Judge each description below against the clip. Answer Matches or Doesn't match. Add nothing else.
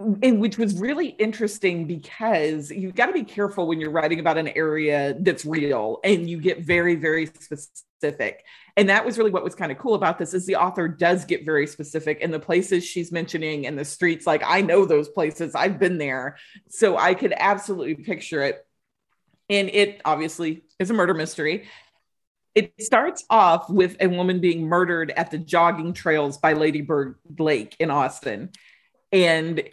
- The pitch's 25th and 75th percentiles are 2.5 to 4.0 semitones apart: Doesn't match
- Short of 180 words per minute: Doesn't match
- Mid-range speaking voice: Matches